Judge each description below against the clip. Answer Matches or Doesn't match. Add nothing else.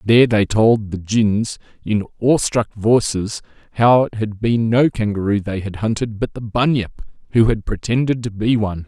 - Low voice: Matches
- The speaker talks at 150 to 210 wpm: Matches